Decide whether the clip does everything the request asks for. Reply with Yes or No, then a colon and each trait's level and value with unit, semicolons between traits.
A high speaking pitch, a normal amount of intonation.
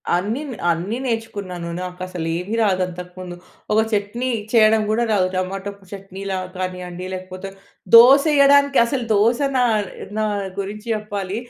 Yes: high, 200 Hz; average, 3.5 semitones